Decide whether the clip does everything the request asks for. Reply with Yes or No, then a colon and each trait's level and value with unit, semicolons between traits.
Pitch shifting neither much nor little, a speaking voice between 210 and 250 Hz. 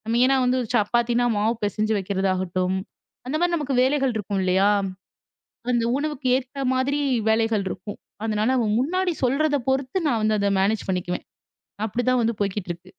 Yes: average, 4.6 semitones; high, 230 Hz